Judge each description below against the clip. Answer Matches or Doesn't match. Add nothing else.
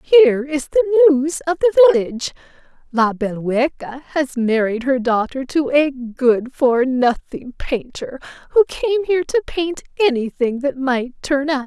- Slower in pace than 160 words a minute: Matches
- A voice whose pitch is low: Doesn't match